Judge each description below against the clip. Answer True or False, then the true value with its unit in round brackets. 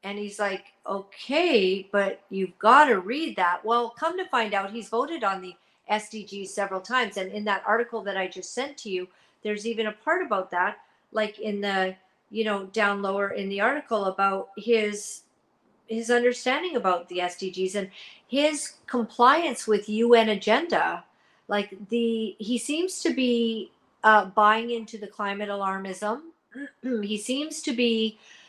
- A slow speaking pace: False (160 wpm)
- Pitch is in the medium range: False (215 Hz)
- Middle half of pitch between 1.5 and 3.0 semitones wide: False (3.4 semitones)